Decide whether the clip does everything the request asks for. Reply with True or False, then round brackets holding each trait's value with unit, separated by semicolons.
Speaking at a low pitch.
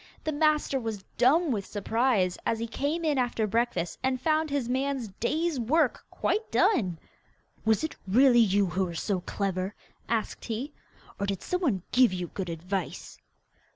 False (235 Hz)